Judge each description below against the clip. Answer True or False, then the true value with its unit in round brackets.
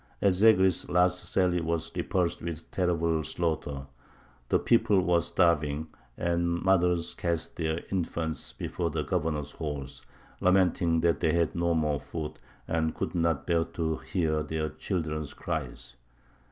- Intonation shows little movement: True (2.0 semitones)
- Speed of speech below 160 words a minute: True (140 wpm)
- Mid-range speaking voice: False (85 Hz)